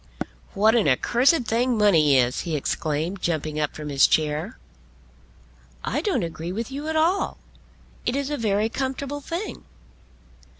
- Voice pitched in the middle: No, high, 210 Hz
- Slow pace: No, average, 145 wpm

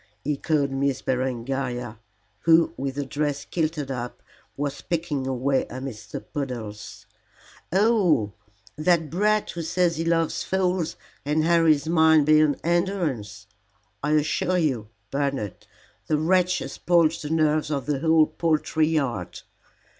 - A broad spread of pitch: No, average, 3.6 semitones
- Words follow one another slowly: Yes, slow, 130 wpm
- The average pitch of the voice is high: No, medium, 150 Hz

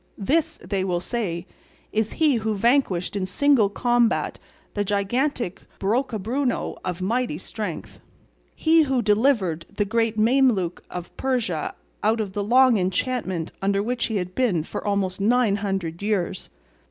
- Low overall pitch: No, high, 210 Hz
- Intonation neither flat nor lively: Yes, average, 4.7 semitones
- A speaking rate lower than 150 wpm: Yes, average, 140 wpm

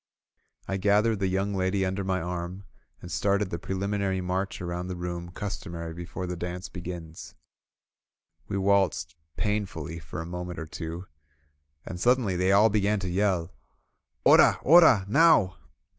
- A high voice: No, very low, 95 Hz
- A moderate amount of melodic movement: No, narrow, 2.3 semitones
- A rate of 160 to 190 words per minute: No, average, 150 wpm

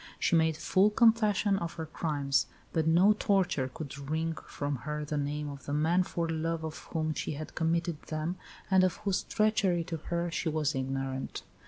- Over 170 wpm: Yes, average, 185 wpm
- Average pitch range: Yes, average, 3.1 semitones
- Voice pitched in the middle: Yes, medium, 160 Hz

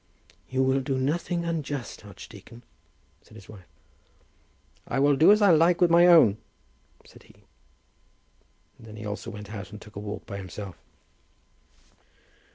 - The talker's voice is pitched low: Yes, low, 130 Hz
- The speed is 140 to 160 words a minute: Yes, average, 155 wpm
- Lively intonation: Yes, wide, 7.9 semitones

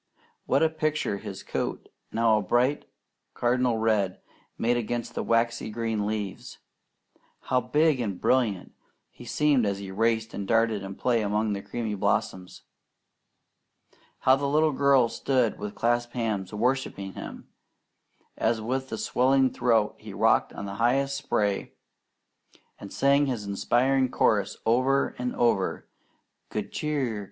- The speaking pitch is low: Yes, low, 115 Hz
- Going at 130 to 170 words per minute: Yes, average, 140 wpm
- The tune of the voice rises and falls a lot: No, average, 3.8 semitones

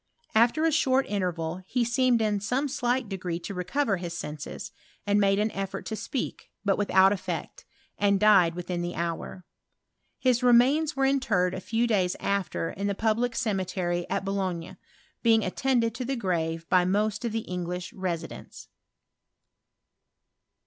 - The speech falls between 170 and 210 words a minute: No, average, 155 wpm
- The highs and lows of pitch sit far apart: No, average, 4.6 semitones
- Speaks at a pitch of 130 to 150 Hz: No, high, 200 Hz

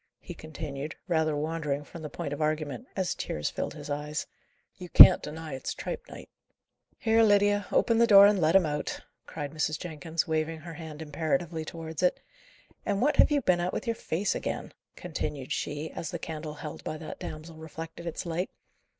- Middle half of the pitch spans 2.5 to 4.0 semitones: Yes, average, 2.8 semitones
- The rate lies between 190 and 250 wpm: Yes, average, 195 wpm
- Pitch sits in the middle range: Yes, medium, 160 Hz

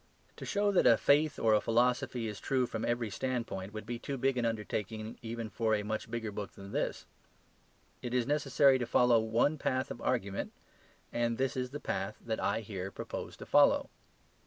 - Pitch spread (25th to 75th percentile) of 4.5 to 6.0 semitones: No, average, 2.9 semitones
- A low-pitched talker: Yes, low, 115 Hz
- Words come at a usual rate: Yes, average, 195 wpm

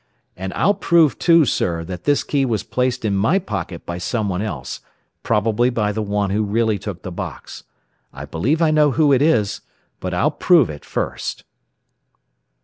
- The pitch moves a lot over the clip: Yes, wide, 6.3 semitones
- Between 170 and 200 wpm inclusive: Yes, average, 175 wpm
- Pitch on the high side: No, low, 110 Hz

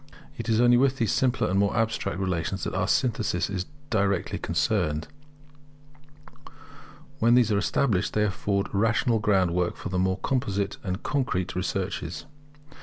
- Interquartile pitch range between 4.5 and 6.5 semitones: No, average, 3.5 semitones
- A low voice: Yes, low, 100 Hz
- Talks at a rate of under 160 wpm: Yes, average, 150 wpm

